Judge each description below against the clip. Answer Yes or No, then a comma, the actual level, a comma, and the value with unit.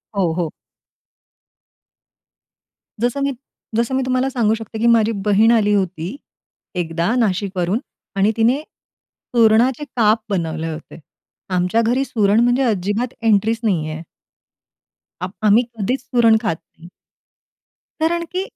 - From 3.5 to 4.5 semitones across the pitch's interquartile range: Yes, average, 4.2 semitones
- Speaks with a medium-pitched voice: No, high, 220 Hz